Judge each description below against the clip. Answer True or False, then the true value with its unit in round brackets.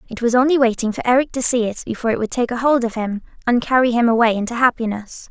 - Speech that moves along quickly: True (250 wpm)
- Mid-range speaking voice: False (235 Hz)